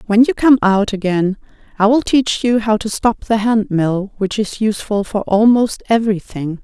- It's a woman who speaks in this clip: Yes, female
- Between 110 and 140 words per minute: No, average, 190 wpm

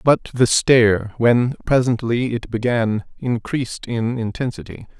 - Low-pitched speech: Yes, low, 120 Hz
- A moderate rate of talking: No, slow, 120 wpm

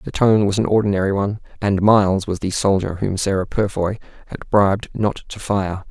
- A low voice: Yes, low, 100 Hz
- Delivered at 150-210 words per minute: Yes, average, 195 wpm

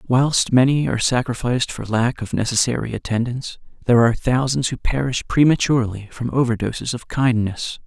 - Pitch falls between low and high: No, low, 125 Hz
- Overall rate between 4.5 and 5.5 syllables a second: No, 5.7 syllables/s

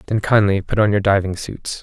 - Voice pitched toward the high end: No, low, 100 Hz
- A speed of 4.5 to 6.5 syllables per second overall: Yes, 5.5 syllables/s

